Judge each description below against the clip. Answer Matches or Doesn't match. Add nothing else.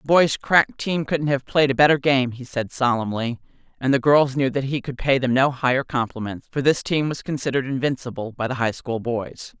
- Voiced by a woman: Matches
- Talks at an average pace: Doesn't match